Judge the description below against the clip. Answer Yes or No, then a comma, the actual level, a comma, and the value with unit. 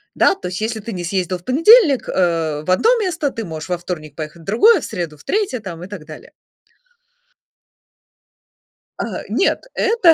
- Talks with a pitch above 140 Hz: Yes, medium, 185 Hz